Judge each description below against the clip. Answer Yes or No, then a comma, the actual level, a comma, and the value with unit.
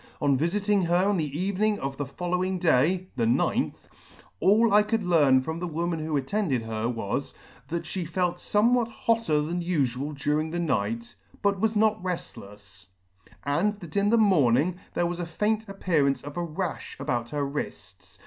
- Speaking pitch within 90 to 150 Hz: No, medium, 170 Hz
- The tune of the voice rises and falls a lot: Yes, wide, 5.9 semitones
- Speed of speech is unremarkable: Yes, average, 175 wpm